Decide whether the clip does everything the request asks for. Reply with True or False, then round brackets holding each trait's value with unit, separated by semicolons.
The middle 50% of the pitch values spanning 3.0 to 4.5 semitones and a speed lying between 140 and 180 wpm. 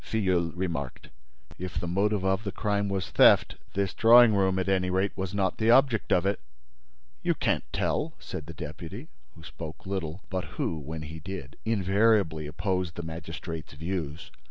True (3.5 semitones; 170 wpm)